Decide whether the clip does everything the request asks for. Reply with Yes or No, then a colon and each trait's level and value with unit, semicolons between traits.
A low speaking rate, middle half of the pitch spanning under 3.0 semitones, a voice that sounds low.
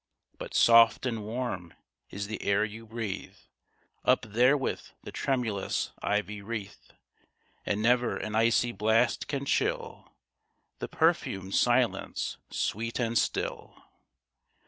Yes: slow, 115 wpm; narrow, 2.4 semitones; low, 115 Hz